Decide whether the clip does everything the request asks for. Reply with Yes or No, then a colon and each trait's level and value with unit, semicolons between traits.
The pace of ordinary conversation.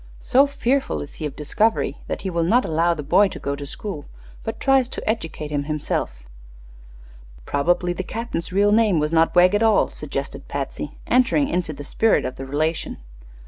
Yes: average, 185 wpm